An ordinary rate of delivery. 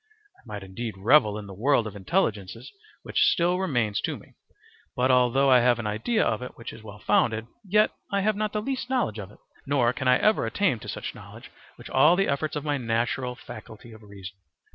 No: fast, 215 wpm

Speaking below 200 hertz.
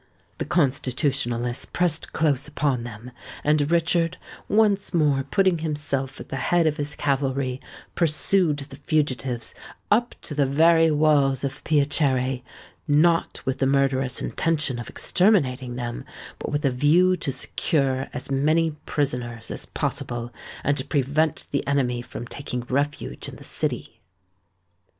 Yes: medium, 140 Hz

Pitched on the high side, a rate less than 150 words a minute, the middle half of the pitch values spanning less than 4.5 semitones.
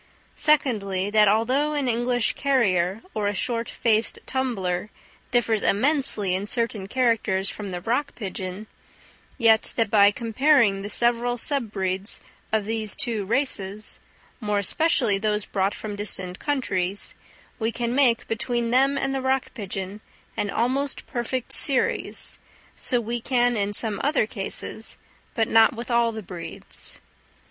Yes: high, 225 Hz; average, 140 wpm; average, 3.6 semitones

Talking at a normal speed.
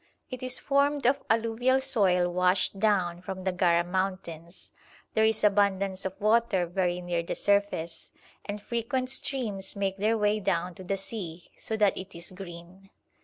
Yes: average, 165 wpm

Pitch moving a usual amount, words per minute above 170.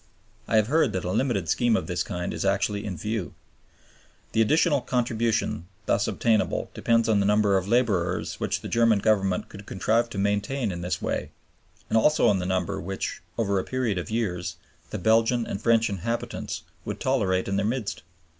Yes: average, 3.4 semitones; average, 185 wpm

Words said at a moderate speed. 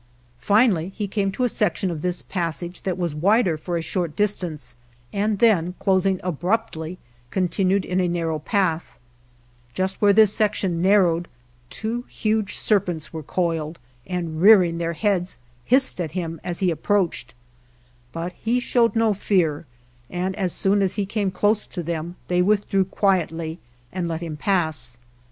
Yes: average, 160 wpm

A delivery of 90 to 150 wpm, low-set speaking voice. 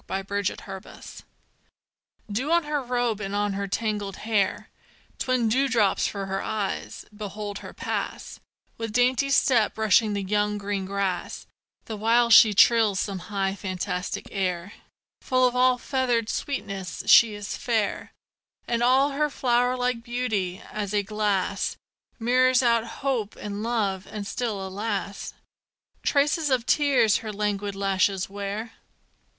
No: average, 140 wpm; high, 215 Hz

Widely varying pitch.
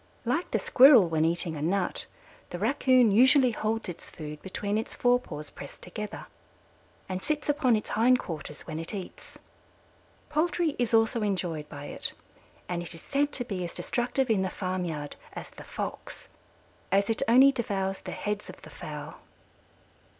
Yes: wide, 6.0 semitones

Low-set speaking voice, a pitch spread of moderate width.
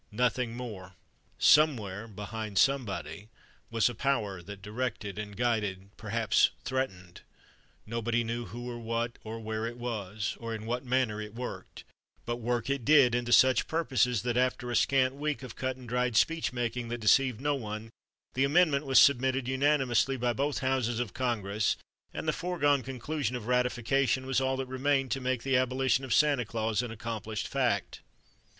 Yes: low, 120 Hz; average, 3.0 semitones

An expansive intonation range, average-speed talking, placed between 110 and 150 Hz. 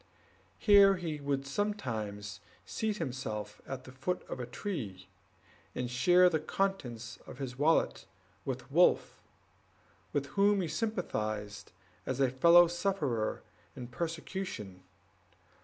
No: wide, 7.4 semitones; slow, 120 wpm; low, 135 Hz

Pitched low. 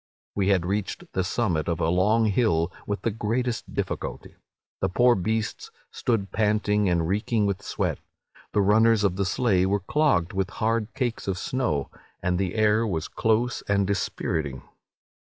Yes: low, 100 Hz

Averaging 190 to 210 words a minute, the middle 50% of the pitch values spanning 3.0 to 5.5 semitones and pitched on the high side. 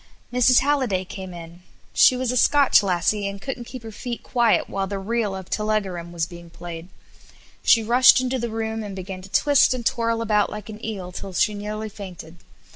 Yes: average, 200 wpm; average, 4.0 semitones; high, 210 Hz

